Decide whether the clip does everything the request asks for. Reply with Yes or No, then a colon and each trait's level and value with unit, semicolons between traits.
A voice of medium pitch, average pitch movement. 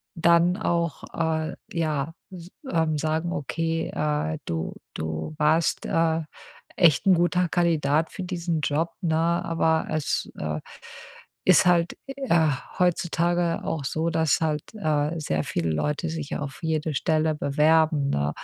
No: medium, 160 Hz; narrow, 2.2 semitones